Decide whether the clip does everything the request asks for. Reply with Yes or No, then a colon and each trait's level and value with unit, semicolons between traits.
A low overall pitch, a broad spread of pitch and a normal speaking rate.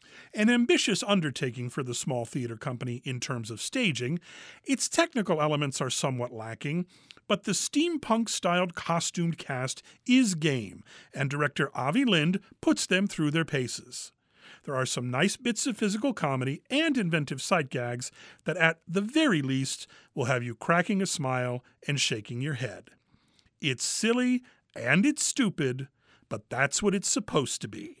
No: medium, 160 Hz; wide, 8.2 semitones; average, 160 wpm